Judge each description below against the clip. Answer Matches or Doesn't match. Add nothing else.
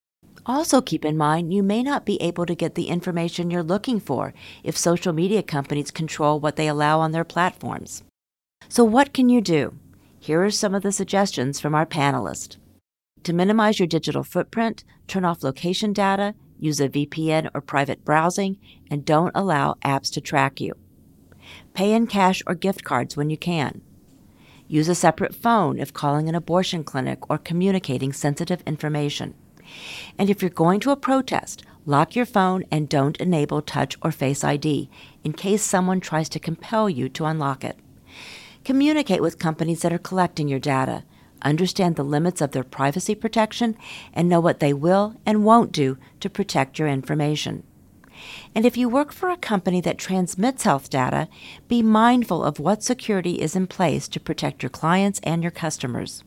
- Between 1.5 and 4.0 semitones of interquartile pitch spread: Doesn't match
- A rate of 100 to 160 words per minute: Doesn't match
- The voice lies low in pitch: Doesn't match